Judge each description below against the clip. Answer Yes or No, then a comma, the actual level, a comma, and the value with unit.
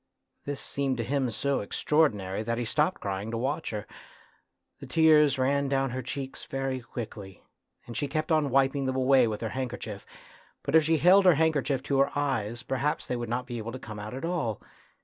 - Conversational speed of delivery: No, fast, 210 wpm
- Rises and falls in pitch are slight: No, average, 3.6 semitones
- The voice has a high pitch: No, low, 130 Hz